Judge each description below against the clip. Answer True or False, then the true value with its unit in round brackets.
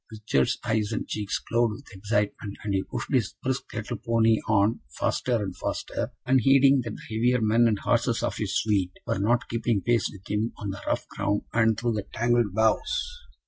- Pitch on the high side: False (110 Hz)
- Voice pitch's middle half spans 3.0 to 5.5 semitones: False (2.6 semitones)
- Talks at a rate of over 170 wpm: True (190 wpm)